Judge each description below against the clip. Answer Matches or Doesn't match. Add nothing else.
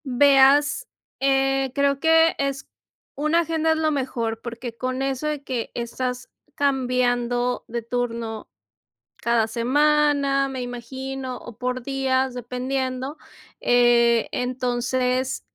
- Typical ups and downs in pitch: Doesn't match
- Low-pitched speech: Doesn't match